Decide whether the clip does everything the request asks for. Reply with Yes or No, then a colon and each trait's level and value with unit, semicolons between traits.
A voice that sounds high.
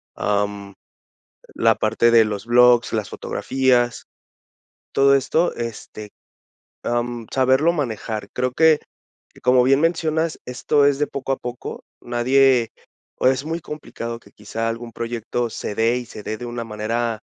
No: low, 120 Hz